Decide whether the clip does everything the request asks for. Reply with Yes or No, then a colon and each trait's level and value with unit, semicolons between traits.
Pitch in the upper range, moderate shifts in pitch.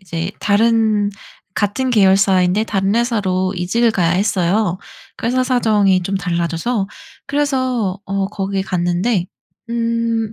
Yes: high, 200 Hz; average, 3.8 semitones